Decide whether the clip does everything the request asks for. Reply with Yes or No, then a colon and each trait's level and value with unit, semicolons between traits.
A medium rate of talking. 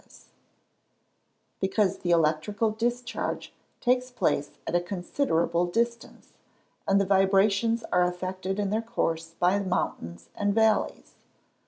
No: slow, 120 wpm